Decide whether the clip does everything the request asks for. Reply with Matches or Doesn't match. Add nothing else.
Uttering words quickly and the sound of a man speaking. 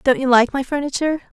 Doesn't match